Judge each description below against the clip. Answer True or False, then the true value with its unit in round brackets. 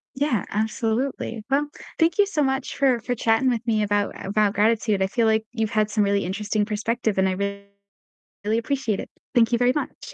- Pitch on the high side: True (220 Hz)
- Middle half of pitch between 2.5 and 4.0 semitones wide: True (3.2 semitones)